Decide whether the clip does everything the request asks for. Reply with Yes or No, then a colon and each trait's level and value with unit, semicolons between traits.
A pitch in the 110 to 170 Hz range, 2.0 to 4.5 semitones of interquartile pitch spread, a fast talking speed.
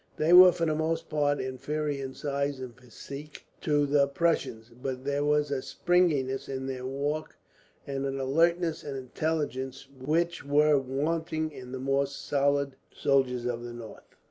No: medium, 140 Hz; narrow, 2.5 semitones; average, 160 wpm